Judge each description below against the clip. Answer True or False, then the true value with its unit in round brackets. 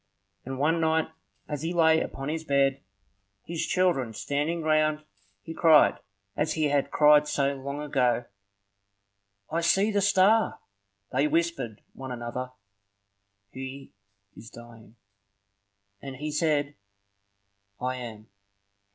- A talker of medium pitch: True (150 Hz)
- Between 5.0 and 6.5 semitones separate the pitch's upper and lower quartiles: False (3.4 semitones)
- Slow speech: True (120 wpm)